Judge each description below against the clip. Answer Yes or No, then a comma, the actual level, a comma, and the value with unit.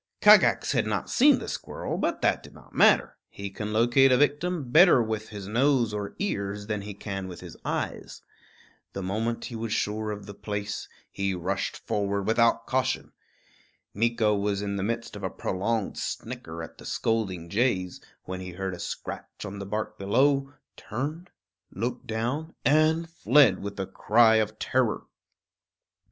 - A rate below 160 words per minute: No, average, 170 wpm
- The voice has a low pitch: Yes, low, 110 Hz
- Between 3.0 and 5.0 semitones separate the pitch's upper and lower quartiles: Yes, average, 3.4 semitones